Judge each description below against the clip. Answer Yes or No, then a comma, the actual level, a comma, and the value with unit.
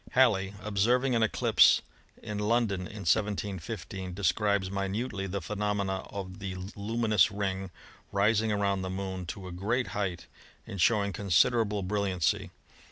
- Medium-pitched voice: No, low, 100 Hz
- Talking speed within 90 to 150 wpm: Yes, slow, 135 wpm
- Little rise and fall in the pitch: Yes, narrow, 1.9 semitones